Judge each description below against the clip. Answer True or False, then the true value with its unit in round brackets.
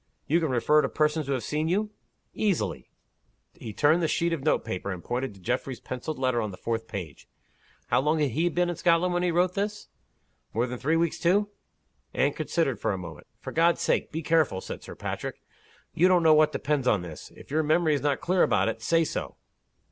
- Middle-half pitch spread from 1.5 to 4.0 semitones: False (5.5 semitones)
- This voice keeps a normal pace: False (220 wpm)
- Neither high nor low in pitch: True (150 Hz)